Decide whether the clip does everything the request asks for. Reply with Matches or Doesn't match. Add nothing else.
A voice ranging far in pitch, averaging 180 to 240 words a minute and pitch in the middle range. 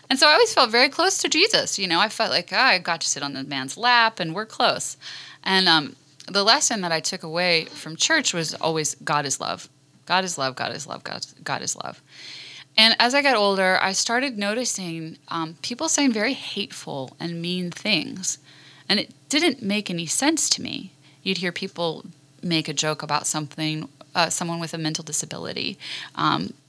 Matches